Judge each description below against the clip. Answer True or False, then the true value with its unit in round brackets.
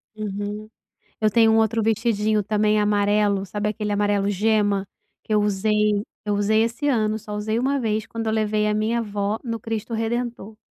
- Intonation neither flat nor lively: False (1.3 semitones)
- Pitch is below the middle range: False (215 Hz)